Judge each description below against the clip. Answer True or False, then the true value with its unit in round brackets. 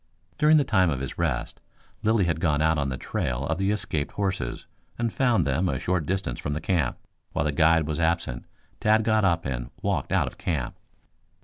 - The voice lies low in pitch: True (80 Hz)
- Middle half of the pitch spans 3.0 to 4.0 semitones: False (5.2 semitones)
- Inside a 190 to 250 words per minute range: True (205 wpm)